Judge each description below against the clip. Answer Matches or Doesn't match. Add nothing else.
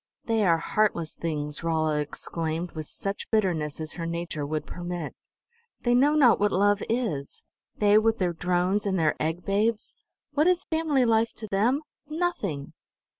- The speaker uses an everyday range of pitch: Doesn't match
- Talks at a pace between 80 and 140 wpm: Doesn't match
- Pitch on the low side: Doesn't match